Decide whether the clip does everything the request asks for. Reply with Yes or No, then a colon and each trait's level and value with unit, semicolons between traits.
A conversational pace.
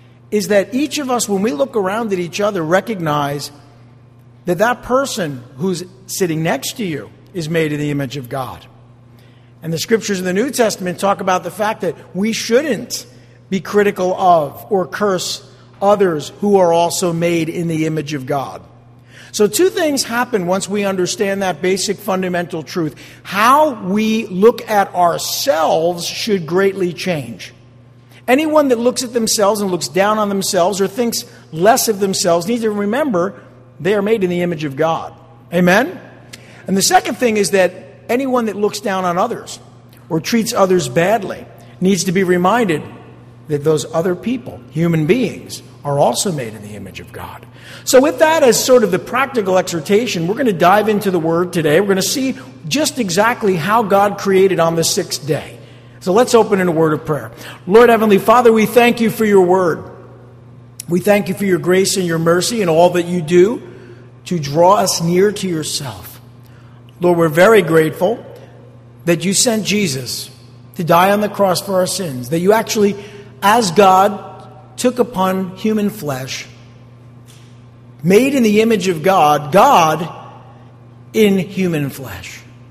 Yes: average, 175 wpm